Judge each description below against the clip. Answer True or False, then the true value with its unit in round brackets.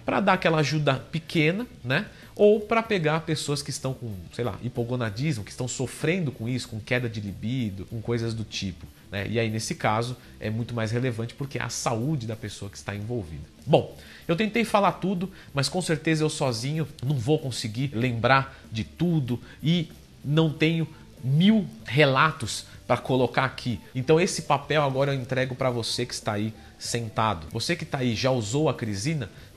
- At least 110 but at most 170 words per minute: False (185 wpm)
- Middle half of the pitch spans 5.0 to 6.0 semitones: True (5.4 semitones)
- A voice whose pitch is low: True (130 Hz)